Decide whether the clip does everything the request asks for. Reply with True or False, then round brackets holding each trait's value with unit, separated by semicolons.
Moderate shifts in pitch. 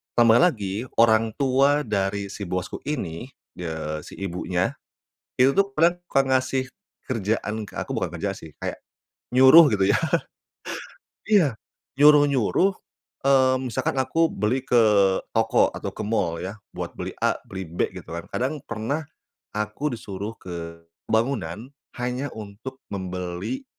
False (5.8 semitones)